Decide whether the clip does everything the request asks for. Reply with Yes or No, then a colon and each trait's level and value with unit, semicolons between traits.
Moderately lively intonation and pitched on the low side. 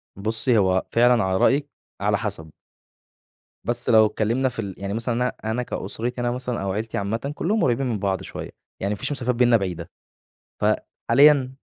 Yes: average, 3.9 semitones; low, 115 Hz